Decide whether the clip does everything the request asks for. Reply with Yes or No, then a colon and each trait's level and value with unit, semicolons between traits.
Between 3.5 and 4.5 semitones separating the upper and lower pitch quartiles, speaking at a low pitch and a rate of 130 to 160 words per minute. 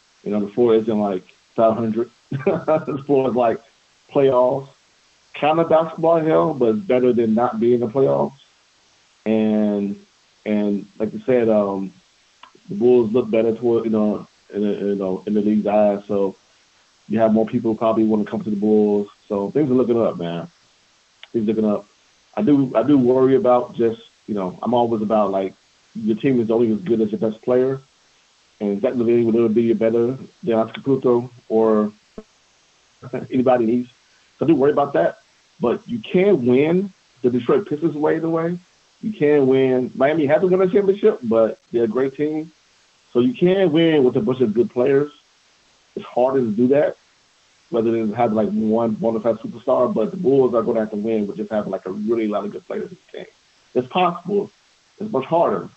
No: average, 3.8 semitones; low, 115 Hz; average, 195 wpm